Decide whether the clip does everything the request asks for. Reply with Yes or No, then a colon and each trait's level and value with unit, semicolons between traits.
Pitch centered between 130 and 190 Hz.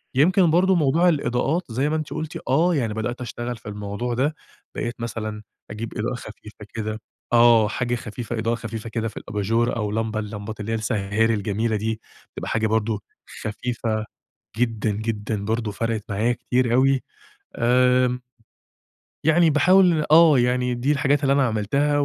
No: low, 115 Hz